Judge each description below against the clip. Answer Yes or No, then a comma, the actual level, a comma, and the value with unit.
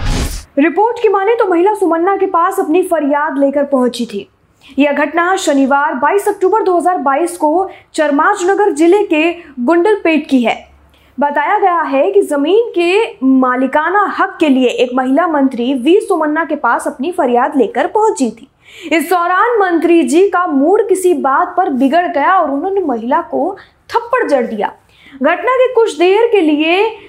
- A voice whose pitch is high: Yes, very high, 340 Hz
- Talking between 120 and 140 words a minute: No, average, 160 wpm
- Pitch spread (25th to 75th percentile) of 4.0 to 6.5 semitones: Yes, average, 5.1 semitones